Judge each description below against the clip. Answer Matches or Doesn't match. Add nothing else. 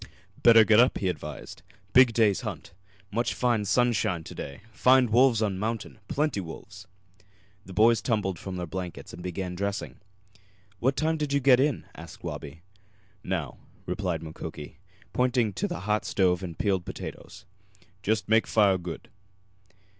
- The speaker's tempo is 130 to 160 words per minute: Matches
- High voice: Doesn't match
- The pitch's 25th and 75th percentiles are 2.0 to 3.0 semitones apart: Doesn't match